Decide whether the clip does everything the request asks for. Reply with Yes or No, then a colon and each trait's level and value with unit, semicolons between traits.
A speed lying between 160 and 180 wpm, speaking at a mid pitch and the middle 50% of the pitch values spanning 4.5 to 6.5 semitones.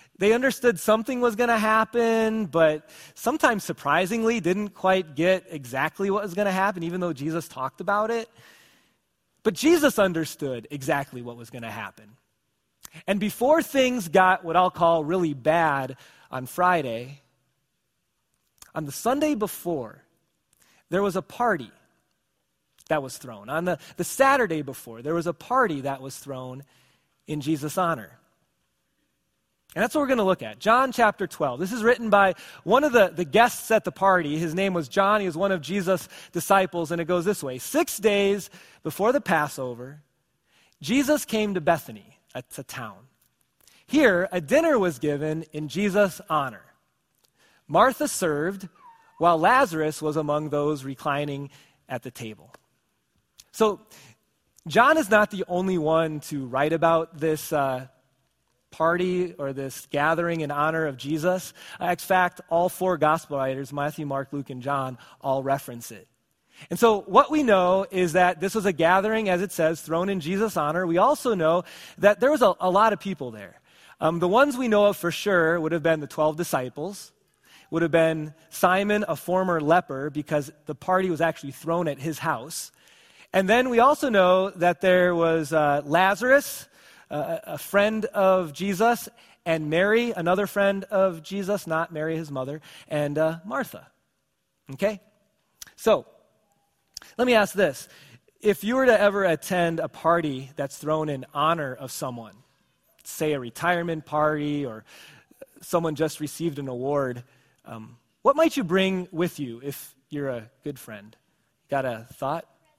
Yes: average, 165 wpm; medium, 170 Hz; average, 5.3 semitones